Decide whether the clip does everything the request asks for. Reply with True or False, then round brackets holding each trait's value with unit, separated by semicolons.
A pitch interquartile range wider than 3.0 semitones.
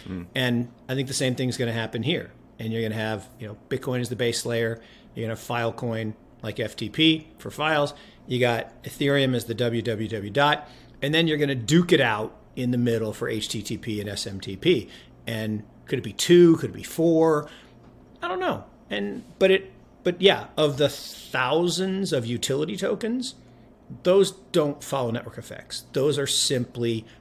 True (4.5 semitones)